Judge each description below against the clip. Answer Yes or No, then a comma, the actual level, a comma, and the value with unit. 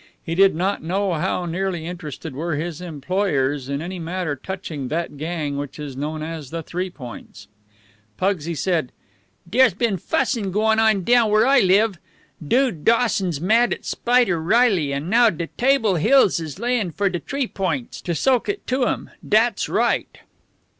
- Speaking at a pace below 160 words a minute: No, average, 165 wpm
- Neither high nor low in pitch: Yes, medium, 180 Hz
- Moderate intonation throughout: No, wide, 5.8 semitones